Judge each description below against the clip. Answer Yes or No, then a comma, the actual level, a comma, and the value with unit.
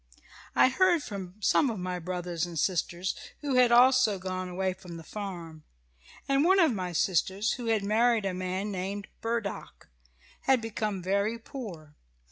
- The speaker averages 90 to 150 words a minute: No, average, 160 wpm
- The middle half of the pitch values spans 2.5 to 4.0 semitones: No, average, 4.4 semitones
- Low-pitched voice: No, high, 200 Hz